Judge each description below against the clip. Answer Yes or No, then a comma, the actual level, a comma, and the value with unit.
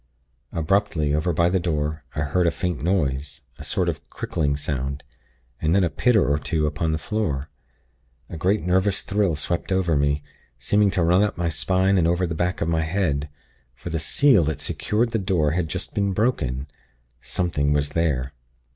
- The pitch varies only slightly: No, average, 4.1 semitones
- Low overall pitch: Yes, very low, 85 Hz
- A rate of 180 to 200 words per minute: Yes, average, 185 wpm